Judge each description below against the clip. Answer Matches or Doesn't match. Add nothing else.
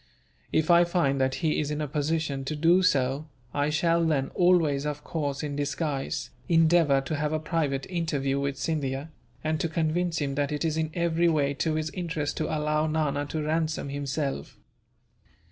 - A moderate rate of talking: Matches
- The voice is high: Doesn't match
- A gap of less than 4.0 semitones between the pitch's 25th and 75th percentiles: Matches